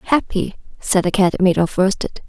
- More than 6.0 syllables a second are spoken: No, 4.8 syllables/s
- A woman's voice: Yes, female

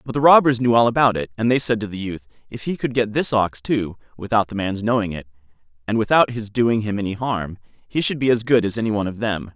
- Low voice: Yes, low, 110 Hz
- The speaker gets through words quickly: Yes, fast, 265 wpm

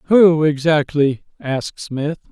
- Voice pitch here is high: No, medium, 150 Hz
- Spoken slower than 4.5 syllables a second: Yes, 3.8 syllables/s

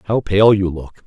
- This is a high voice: No, low, 100 Hz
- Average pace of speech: No, fast, 225 wpm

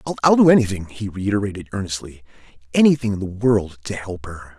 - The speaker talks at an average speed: Yes, average, 155 wpm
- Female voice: No, male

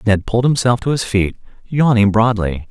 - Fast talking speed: No, average, 180 wpm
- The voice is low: Yes, low, 110 Hz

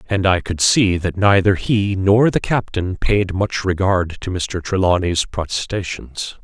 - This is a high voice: No, very low, 95 Hz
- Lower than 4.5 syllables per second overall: Yes, 4.0 syllables/s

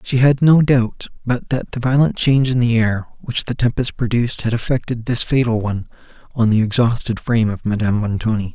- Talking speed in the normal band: Yes, average, 195 wpm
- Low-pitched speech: Yes, low, 120 Hz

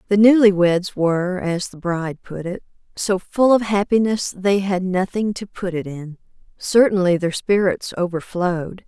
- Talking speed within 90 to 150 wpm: No, average, 160 wpm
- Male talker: No, female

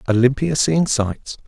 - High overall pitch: No, low, 130 Hz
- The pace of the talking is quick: No, slow, 120 wpm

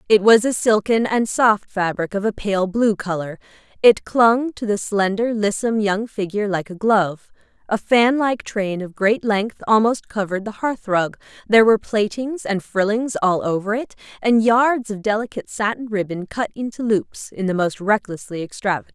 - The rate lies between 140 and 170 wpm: No, average, 185 wpm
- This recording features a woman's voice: Yes, female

